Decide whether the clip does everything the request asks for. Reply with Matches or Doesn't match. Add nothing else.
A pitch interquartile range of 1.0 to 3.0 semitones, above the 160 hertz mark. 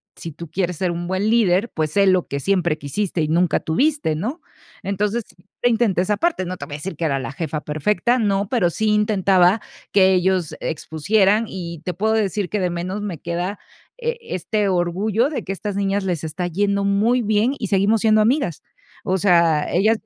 Doesn't match